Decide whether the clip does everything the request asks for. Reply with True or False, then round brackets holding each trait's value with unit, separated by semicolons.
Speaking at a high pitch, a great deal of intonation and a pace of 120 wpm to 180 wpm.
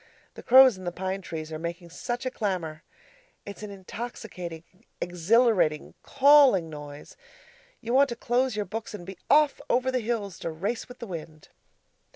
True (200 Hz; 6.1 semitones; 170 wpm)